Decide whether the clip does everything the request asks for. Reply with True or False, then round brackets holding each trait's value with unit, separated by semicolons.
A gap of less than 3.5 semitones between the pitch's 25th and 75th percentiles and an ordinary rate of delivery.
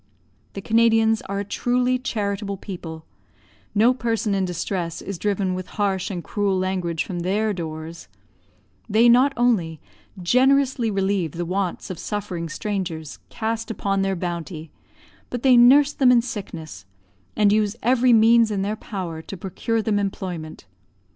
False (4.1 semitones; 150 wpm)